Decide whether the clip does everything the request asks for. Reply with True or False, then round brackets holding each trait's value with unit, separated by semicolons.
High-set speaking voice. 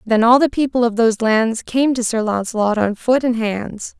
True (230 Hz)